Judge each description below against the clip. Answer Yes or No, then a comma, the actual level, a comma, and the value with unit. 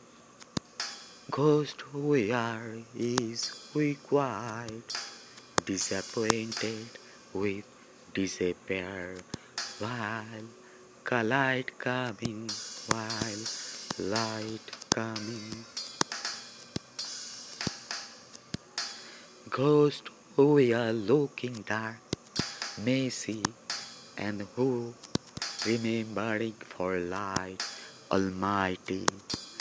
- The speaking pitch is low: Yes, low, 115 Hz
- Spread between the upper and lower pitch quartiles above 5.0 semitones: No, average, 2.9 semitones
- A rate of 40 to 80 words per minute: Yes, average, 60 wpm